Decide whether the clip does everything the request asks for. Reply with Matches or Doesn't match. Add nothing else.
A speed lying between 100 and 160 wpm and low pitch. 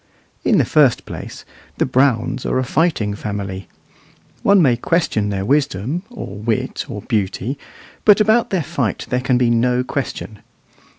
Matches